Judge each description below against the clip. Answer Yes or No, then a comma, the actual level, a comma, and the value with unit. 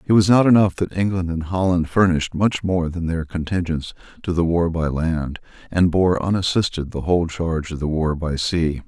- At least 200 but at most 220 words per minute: Yes, fast, 205 wpm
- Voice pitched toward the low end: Yes, very low, 85 Hz